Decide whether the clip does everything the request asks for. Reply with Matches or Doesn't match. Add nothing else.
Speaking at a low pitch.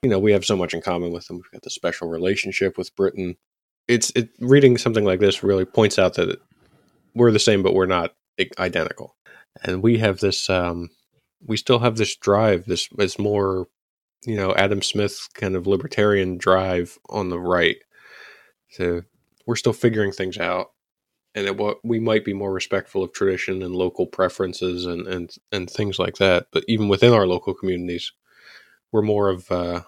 Matches